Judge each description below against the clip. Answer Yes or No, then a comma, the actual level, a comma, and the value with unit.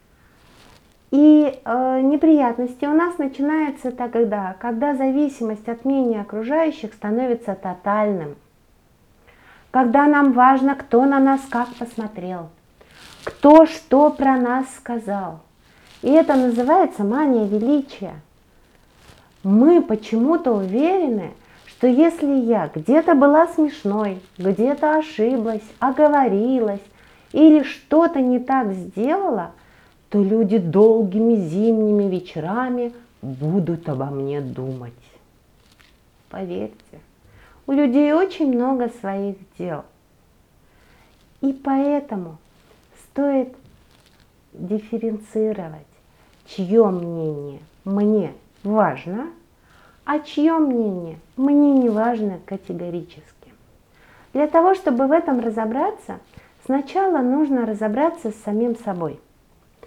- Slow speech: Yes, slow, 90 wpm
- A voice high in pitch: Yes, high, 235 Hz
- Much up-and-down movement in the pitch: Yes, wide, 6.1 semitones